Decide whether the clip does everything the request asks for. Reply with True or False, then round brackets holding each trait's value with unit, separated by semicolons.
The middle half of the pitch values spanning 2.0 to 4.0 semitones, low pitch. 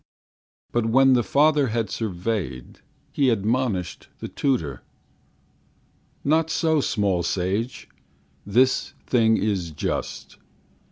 False (5.6 semitones; 115 Hz)